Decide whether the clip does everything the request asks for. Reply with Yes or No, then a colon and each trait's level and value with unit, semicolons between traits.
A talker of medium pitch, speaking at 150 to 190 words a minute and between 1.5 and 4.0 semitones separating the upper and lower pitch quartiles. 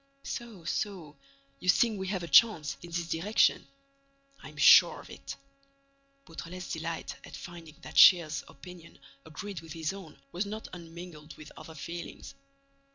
No: medium, 170 Hz; slow, 135 wpm; average, 2.7 semitones